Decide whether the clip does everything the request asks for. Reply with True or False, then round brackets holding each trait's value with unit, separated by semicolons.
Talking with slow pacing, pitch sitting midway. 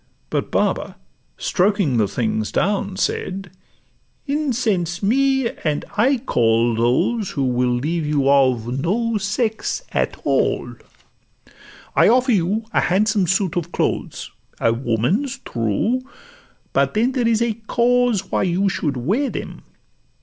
False (130 wpm; 195 Hz)